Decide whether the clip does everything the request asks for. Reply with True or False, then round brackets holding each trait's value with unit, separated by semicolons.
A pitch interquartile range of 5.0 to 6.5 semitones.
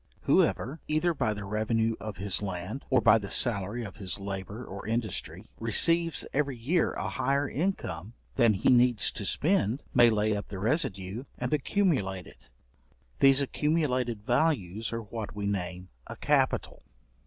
True (5.3 semitones)